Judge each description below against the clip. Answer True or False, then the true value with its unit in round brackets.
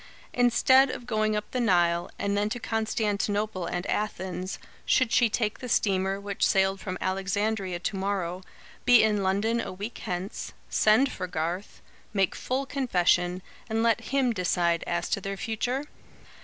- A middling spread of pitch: True (3.3 semitones)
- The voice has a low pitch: False (200 Hz)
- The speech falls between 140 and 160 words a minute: True (155 wpm)